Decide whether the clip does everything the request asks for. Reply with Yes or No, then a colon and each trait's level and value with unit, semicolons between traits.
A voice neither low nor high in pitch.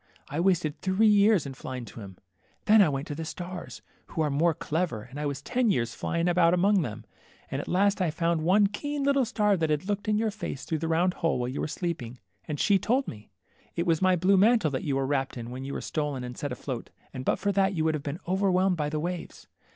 Yes: medium, 165 Hz